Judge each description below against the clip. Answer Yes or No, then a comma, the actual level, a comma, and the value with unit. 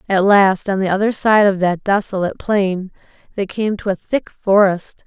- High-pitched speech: Yes, high, 195 Hz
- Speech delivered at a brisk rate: No, average, 190 wpm